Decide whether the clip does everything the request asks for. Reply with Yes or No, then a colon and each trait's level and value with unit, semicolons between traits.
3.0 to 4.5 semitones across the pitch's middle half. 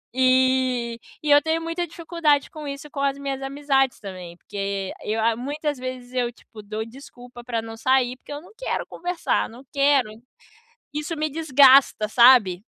Yes: average, 3.7 semitones